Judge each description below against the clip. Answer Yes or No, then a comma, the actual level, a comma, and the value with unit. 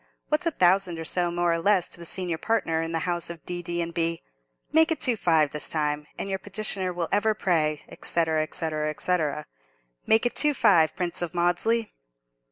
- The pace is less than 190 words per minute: No, average, 200 wpm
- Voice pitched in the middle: Yes, medium, 175 Hz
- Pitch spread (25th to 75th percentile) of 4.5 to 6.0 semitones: No, average, 3.4 semitones